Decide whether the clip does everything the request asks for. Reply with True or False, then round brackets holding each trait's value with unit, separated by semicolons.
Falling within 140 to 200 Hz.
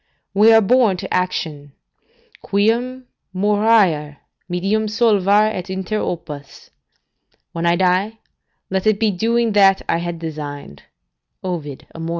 True (190 Hz)